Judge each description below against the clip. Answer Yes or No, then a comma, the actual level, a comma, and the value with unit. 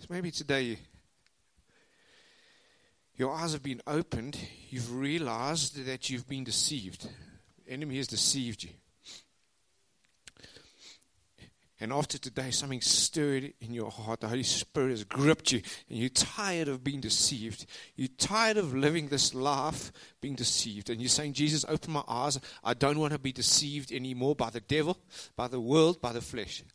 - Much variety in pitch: No, average, 3.7 semitones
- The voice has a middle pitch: No, low, 130 Hz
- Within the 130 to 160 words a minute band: Yes, average, 155 wpm